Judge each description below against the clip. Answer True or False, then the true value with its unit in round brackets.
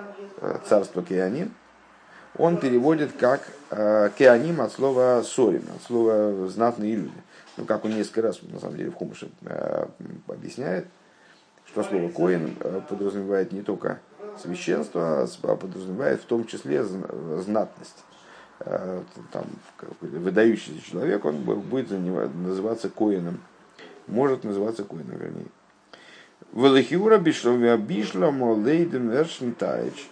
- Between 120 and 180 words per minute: False (110 wpm)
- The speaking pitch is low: True (115 Hz)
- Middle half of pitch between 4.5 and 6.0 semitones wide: True (4.8 semitones)